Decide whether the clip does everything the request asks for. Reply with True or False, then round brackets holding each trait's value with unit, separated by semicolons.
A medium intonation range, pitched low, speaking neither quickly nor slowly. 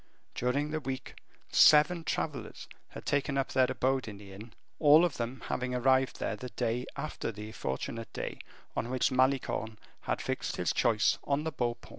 True (3.4 semitones; 130 Hz; 180 wpm)